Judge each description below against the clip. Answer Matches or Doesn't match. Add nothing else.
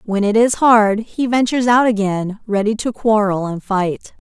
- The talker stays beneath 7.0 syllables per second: Matches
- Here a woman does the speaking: Matches